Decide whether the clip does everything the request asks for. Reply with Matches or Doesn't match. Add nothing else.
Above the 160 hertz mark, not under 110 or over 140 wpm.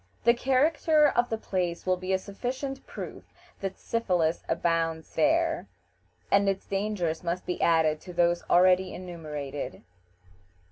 Matches